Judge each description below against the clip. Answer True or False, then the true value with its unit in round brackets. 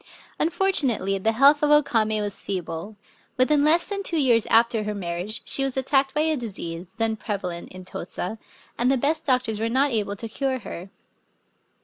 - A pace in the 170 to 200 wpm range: True (180 wpm)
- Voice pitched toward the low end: False (230 Hz)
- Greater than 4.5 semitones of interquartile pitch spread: True (5.5 semitones)